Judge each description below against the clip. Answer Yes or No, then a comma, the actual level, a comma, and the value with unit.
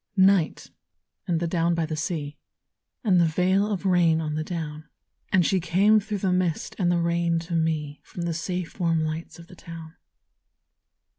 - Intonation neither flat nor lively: No, narrow, 2.2 semitones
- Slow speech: No, average, 180 wpm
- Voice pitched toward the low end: No, medium, 170 Hz